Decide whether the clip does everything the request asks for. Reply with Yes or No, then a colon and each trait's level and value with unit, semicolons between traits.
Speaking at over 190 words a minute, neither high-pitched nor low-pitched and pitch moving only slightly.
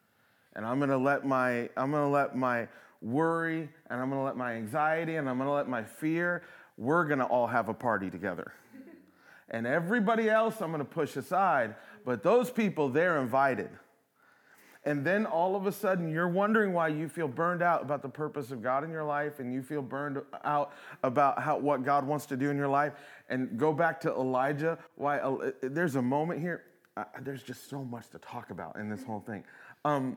No: average, 200 wpm; medium, 145 Hz; average, 3.9 semitones